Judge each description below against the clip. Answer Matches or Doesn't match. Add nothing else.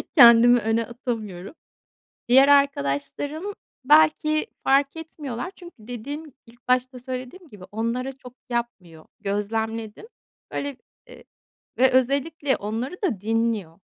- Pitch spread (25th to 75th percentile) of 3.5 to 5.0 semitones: Matches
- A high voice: Matches